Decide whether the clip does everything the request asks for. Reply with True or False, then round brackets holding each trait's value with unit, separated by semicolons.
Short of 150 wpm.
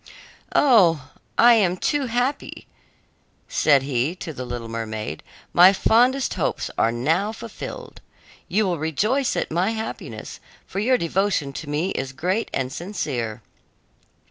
True (135 wpm)